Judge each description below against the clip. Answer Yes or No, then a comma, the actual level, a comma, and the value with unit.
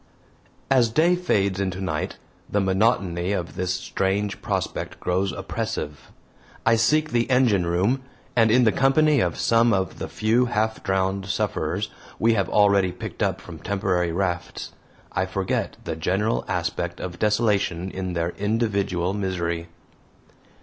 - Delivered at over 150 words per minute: No, average, 145 wpm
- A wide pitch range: No, average, 3.7 semitones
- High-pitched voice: No, low, 100 Hz